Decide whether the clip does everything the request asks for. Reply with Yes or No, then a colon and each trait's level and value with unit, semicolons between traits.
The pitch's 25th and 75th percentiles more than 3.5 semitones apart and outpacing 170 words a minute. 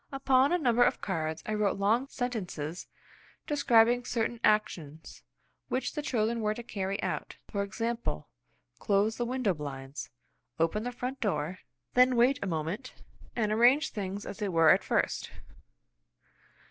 No: average, 4.6 semitones; average, 145 wpm